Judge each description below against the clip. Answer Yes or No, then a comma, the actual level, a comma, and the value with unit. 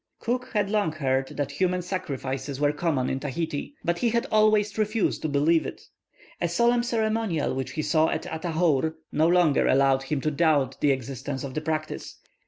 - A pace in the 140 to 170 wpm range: No, average, 185 wpm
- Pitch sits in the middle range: Yes, medium, 155 Hz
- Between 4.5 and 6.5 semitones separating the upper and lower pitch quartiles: Yes, average, 5.1 semitones